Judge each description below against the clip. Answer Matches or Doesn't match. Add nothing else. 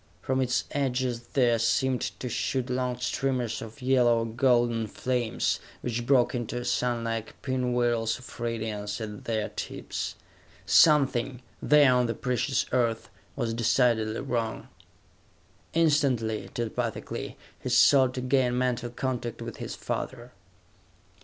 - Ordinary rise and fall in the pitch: Doesn't match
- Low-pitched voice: Matches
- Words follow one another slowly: Matches